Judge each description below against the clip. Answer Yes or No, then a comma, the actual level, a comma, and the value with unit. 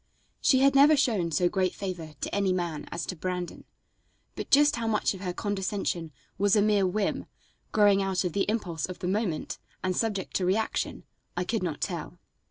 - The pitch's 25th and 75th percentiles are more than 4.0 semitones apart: No, average, 3.0 semitones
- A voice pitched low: No, high, 195 Hz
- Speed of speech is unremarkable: Yes, average, 190 wpm